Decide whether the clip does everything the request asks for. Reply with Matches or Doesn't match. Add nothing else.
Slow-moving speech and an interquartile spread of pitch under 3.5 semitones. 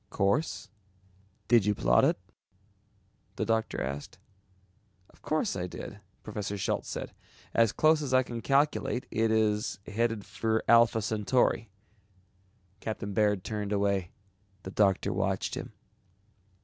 Matches